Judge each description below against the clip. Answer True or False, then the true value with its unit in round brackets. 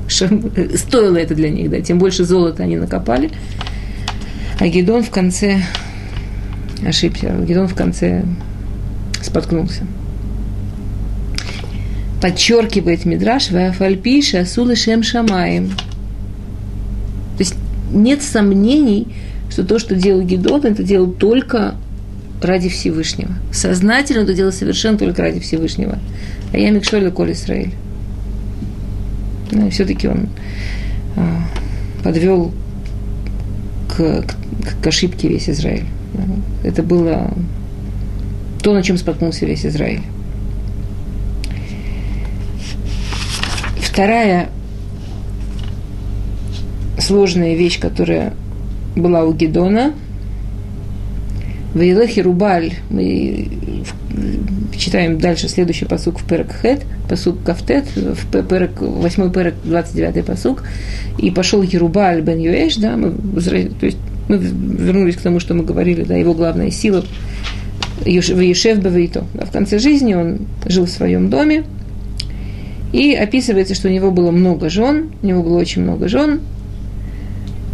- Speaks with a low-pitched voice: True (100 Hz)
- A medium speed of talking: False (105 wpm)